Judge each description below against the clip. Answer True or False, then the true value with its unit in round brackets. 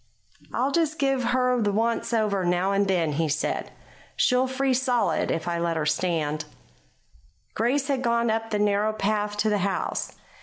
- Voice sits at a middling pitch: False (215 Hz)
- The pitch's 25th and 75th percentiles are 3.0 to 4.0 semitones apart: False (5.6 semitones)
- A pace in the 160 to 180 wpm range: True (175 wpm)